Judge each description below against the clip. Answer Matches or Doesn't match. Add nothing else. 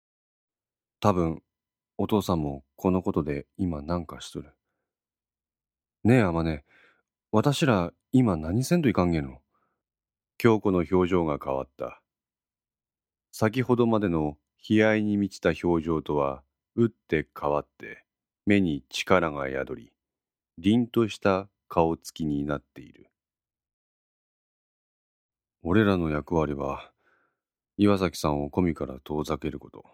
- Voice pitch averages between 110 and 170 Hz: Doesn't match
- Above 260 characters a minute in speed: Doesn't match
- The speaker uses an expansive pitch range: Matches